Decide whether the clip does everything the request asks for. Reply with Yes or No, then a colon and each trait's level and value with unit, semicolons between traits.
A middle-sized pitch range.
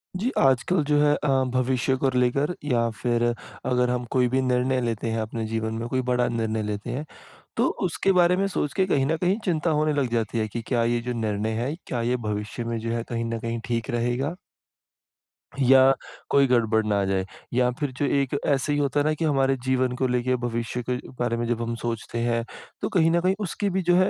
Yes: average, 3.7 semitones